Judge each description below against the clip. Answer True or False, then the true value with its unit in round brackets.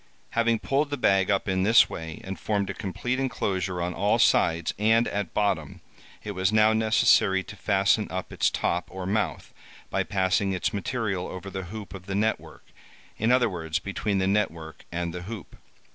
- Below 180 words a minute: False (190 wpm)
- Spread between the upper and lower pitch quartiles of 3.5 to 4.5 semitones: False (2.8 semitones)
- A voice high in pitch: False (100 Hz)